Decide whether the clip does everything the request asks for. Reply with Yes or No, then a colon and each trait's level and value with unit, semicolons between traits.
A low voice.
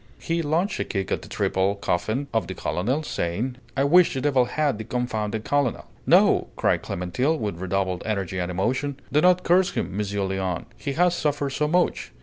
Yes: low, 125 Hz